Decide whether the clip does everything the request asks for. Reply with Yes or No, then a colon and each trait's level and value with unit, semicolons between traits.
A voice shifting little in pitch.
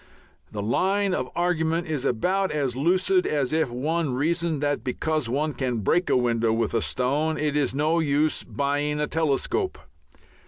No: average, 4.3 semitones